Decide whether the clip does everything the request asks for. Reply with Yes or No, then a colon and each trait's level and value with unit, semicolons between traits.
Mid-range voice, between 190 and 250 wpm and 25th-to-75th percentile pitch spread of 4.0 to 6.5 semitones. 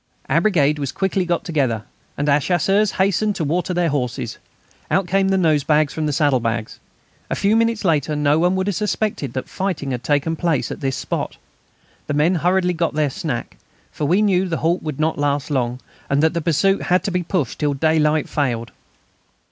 Yes: medium, 160 Hz; average, 195 wpm; average, 4.3 semitones